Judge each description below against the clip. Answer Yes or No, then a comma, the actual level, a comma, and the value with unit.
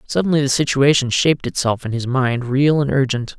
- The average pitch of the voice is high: No, low, 130 Hz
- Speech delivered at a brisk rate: No, average, 195 wpm